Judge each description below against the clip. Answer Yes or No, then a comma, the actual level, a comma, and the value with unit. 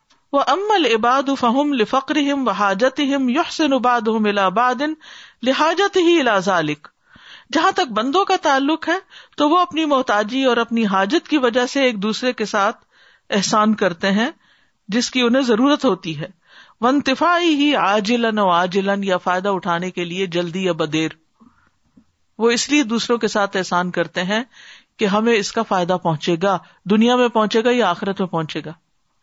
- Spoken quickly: No, average, 165 wpm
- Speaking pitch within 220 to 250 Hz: Yes, high, 230 Hz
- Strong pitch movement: Yes, wide, 5.9 semitones